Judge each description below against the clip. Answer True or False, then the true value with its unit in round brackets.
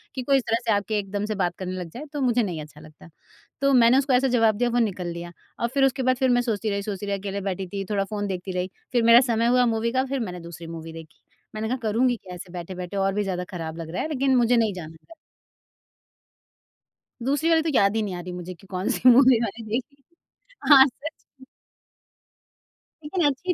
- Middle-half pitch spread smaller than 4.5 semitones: False (5.5 semitones)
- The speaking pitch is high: True (215 Hz)